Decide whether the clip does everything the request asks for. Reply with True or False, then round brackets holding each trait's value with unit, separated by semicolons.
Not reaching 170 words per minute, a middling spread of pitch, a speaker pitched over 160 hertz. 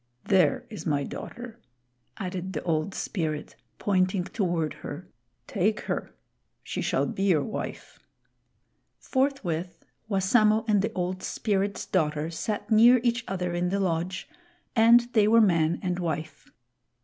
True (135 wpm; 3.9 semitones; 190 Hz)